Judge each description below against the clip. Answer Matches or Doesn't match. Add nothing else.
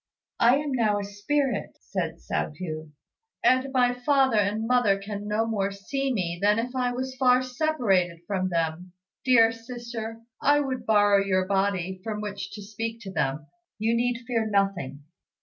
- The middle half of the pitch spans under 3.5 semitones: Doesn't match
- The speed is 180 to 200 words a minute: Doesn't match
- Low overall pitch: Doesn't match